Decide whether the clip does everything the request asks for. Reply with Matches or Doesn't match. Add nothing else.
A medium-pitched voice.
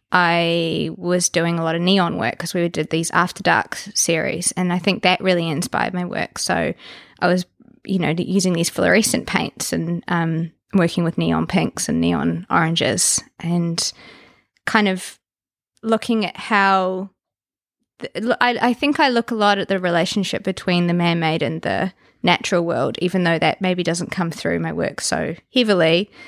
Matches